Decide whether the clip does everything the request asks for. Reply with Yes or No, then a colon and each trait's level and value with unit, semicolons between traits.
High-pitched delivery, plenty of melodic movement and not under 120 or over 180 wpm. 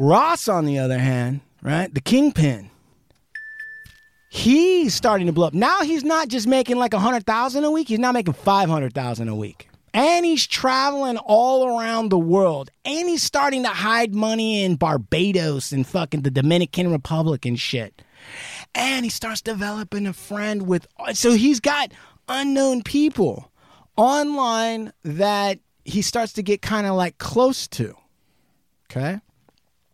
Yes: high, 215 Hz; wide, 7.9 semitones; average, 155 wpm